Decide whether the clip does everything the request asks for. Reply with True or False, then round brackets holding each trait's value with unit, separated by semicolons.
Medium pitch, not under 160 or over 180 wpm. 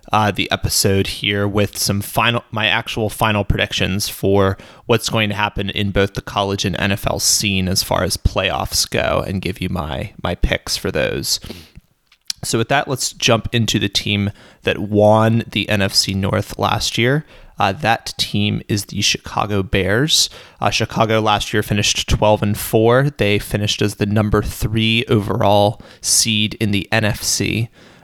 False (105 Hz; 165 wpm)